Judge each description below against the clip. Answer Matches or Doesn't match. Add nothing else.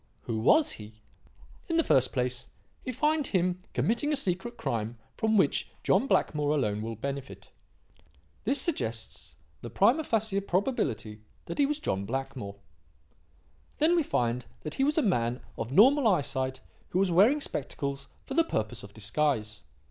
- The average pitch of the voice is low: Doesn't match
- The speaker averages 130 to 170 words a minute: Matches